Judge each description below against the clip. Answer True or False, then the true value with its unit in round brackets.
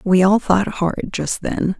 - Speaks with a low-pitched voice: False (190 Hz)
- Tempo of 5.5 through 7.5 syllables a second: False (4.0 syllables/s)